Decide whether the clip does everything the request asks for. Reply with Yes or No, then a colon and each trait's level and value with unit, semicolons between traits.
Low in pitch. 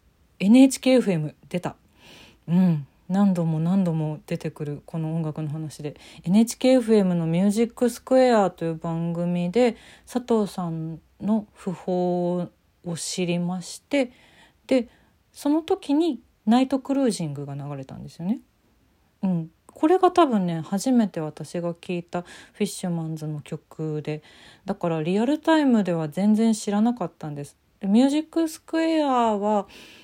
No: medium, 185 Hz